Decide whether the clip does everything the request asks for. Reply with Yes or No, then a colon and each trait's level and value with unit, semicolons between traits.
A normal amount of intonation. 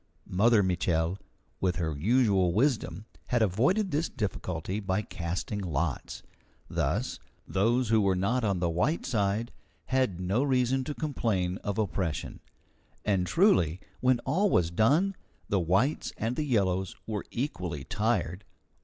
No: wide, 5.7 semitones